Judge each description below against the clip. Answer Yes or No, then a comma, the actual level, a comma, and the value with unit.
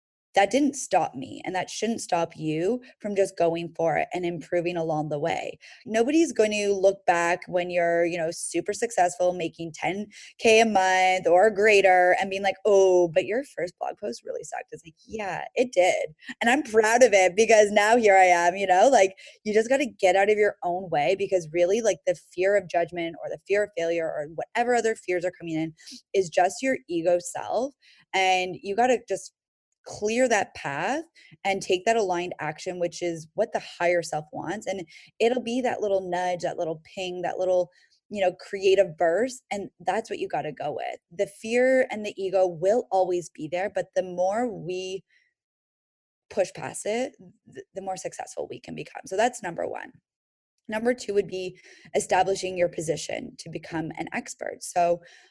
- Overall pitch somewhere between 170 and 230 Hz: Yes, high, 190 Hz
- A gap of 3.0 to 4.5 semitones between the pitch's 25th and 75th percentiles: Yes, average, 3.8 semitones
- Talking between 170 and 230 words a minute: Yes, average, 195 wpm